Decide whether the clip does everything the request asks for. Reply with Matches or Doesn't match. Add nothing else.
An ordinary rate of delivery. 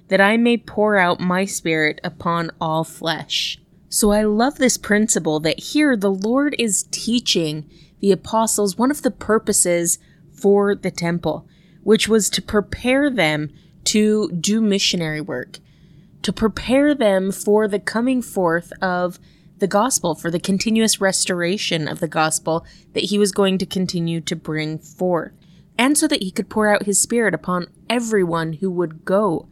Matches